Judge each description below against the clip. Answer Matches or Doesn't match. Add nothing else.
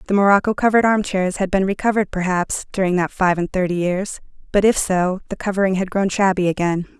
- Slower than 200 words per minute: Doesn't match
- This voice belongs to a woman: Matches